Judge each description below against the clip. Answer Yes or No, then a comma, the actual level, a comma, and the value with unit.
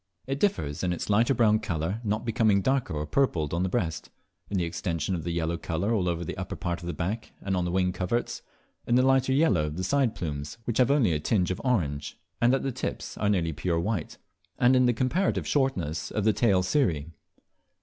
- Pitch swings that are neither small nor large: No, wide, 6.2 semitones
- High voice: No, very low, 95 Hz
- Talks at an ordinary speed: No, fast, 225 wpm